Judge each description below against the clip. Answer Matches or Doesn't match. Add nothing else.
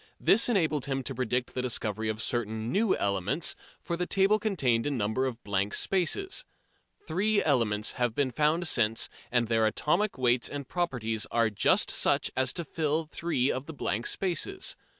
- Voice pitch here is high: Doesn't match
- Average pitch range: Doesn't match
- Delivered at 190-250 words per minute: Doesn't match